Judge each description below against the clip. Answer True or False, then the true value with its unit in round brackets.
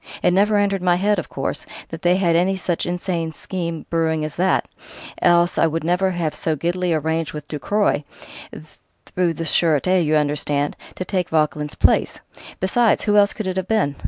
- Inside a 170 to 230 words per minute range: True (185 wpm)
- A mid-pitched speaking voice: True (175 Hz)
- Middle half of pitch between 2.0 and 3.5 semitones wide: True (2.9 semitones)